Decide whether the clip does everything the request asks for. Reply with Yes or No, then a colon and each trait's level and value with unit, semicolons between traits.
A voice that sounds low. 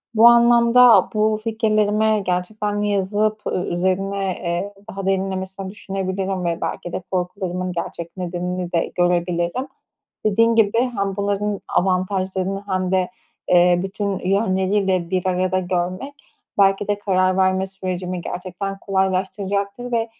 No: high, 190 Hz